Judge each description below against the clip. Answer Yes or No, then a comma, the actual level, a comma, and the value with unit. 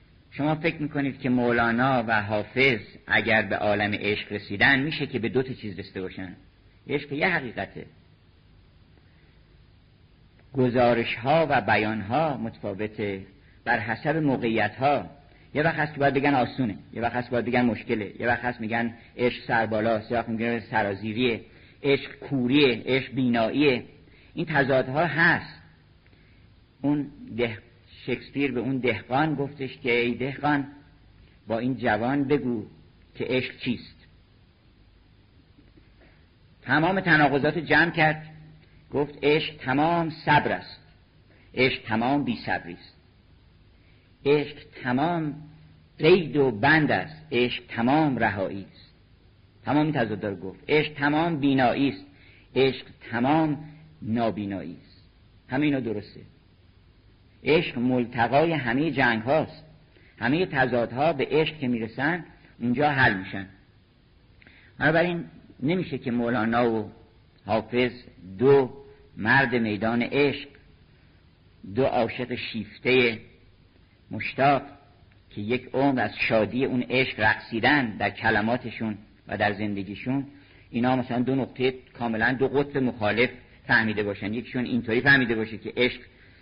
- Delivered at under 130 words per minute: Yes, average, 120 wpm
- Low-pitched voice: Yes, low, 120 Hz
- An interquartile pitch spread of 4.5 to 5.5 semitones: Yes, average, 5.0 semitones